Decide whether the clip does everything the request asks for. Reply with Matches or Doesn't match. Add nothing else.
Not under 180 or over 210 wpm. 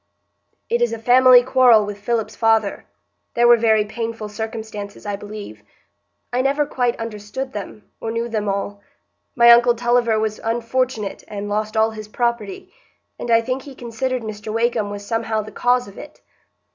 Doesn't match